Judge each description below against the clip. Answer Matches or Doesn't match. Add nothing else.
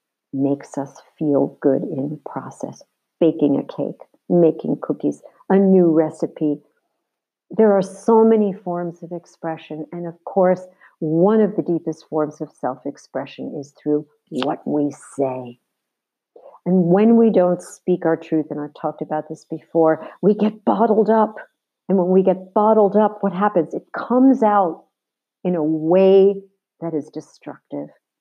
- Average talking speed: Matches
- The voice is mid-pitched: Matches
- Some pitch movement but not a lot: Matches